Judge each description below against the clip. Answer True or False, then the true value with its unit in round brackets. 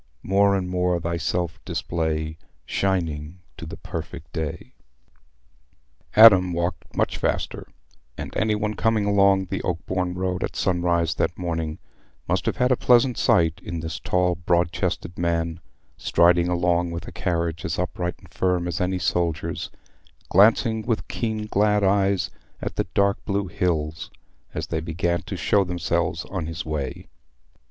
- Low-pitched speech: True (90 Hz)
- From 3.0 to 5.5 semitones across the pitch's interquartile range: False (2.6 semitones)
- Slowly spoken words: False (150 wpm)